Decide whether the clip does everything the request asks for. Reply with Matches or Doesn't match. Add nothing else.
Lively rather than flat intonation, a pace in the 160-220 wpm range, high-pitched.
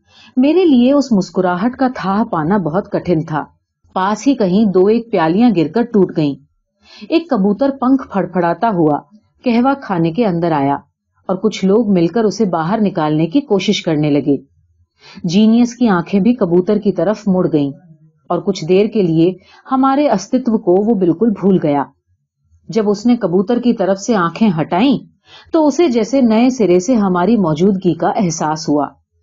Matches